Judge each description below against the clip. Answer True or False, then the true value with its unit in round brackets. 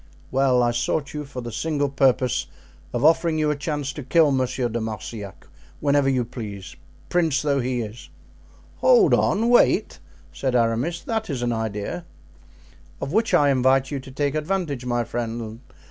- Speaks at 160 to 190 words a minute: True (165 wpm)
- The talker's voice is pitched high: False (135 Hz)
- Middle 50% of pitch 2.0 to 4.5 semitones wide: True (3.8 semitones)